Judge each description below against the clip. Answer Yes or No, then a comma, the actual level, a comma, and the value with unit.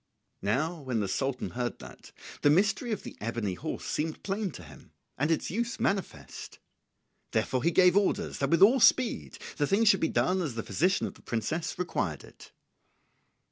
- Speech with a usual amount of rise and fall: No, wide, 7.6 semitones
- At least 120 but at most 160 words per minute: No, average, 180 wpm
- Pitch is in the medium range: Yes, medium, 165 Hz